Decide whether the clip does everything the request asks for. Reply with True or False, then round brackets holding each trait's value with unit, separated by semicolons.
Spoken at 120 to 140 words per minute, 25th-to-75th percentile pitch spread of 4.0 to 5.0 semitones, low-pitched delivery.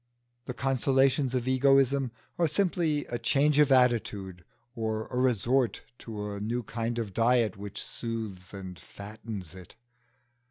True (135 wpm; 4.3 semitones; 120 Hz)